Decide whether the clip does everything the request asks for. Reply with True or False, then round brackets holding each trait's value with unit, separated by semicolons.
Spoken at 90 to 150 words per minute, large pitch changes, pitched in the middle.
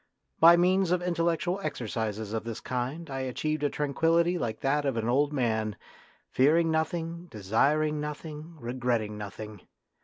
True (145 wpm; 5.9 semitones; 145 Hz)